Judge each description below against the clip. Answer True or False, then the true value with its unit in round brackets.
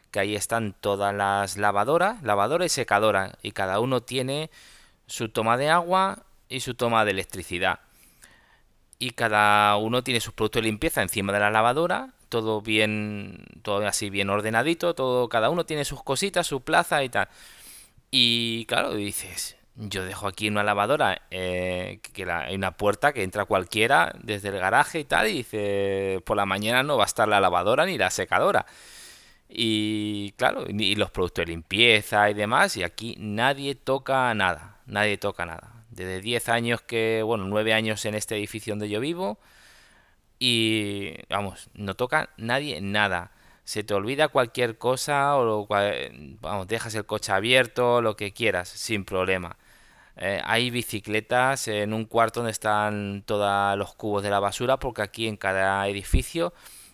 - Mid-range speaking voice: False (105 Hz)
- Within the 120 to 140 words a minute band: False (165 wpm)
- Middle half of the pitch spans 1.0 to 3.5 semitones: True (3.0 semitones)